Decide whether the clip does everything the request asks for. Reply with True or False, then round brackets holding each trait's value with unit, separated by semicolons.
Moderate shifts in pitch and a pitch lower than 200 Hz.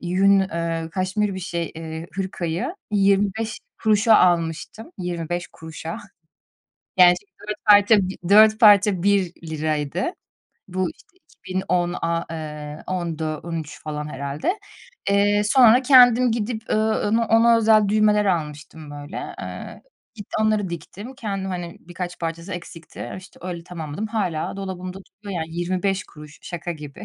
True (3.9 semitones; 185 Hz)